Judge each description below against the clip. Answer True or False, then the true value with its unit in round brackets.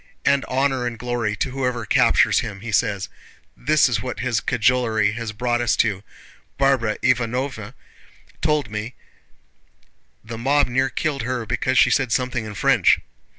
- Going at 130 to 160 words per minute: True (150 wpm)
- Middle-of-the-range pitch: False (120 Hz)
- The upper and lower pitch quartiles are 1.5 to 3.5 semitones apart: True (2.8 semitones)